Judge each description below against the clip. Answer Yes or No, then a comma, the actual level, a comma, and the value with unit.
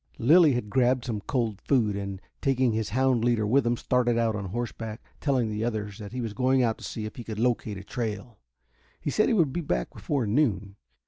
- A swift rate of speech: Yes, fast, 220 wpm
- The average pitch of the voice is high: No, low, 115 Hz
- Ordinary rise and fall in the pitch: Yes, average, 3.3 semitones